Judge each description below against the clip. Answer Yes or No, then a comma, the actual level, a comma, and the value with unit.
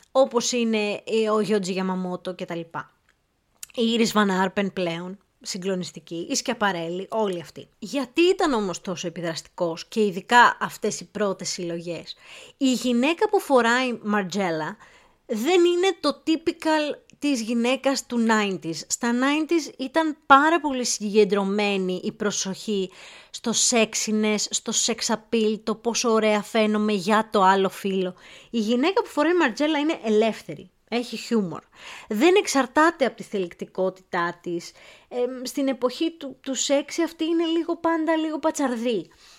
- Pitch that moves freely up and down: Yes, wide, 6.1 semitones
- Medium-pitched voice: No, high, 220 Hz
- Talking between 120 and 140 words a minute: Yes, average, 130 wpm